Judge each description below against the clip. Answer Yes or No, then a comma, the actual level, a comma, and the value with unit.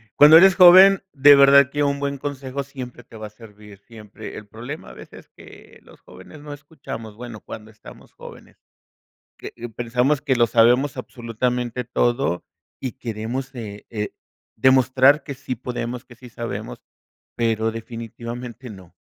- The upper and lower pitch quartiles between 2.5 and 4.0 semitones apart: Yes, average, 3.4 semitones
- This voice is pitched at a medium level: No, low, 125 Hz